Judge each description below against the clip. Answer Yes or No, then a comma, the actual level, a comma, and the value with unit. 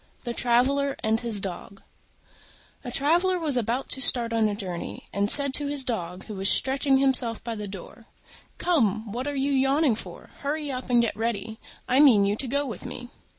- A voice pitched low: No, high, 245 Hz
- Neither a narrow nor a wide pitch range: Yes, average, 4.2 semitones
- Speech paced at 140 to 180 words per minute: No, average, 195 wpm